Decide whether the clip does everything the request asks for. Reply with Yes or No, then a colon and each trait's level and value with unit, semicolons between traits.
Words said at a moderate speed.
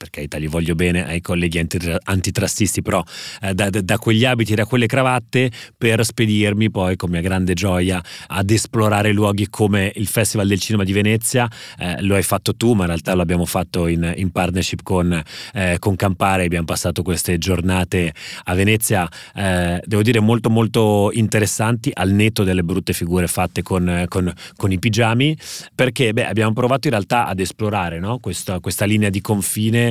No: fast, 180 wpm